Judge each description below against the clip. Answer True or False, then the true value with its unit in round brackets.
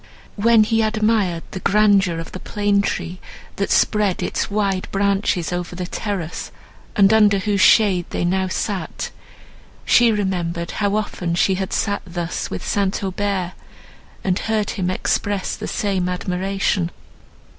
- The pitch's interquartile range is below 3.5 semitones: True (2.4 semitones)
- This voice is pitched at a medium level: False (195 Hz)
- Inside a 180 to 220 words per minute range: False (145 wpm)